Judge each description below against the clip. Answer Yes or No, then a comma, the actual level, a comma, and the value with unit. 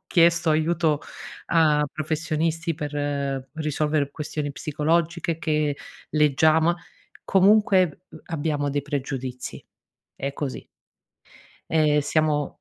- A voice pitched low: No, medium, 155 Hz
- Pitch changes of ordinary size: No, narrow, 2.1 semitones